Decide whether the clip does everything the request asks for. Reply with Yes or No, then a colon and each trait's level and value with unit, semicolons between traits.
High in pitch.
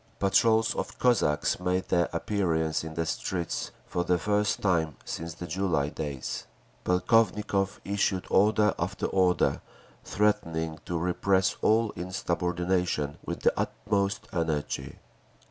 No: very low, 90 Hz